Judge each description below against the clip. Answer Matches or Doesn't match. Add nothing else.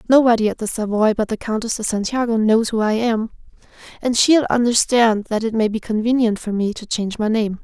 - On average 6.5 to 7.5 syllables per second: Doesn't match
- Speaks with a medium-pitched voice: Doesn't match